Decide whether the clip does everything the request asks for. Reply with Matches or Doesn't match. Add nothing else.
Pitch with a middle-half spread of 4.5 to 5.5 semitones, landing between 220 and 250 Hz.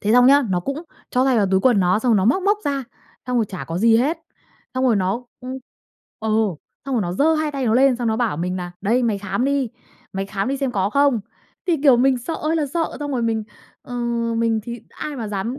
Matches